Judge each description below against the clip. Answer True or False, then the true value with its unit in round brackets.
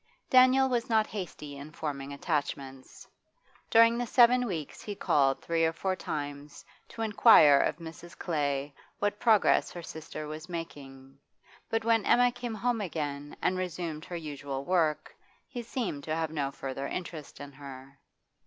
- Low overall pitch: False (160 Hz)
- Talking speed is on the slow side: False (155 wpm)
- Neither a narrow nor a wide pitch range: False (7.1 semitones)